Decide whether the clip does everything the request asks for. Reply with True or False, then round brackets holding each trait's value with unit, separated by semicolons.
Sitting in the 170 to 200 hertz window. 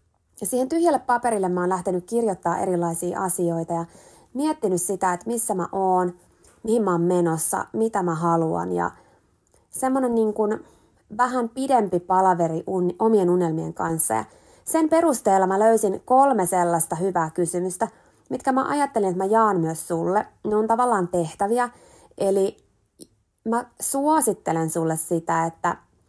True (190 Hz)